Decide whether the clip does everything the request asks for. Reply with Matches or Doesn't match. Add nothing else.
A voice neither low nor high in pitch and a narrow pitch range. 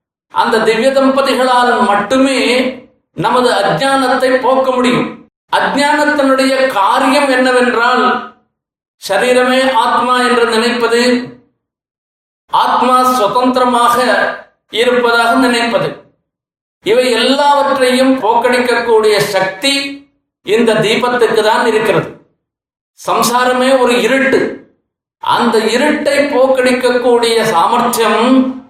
Doesn't match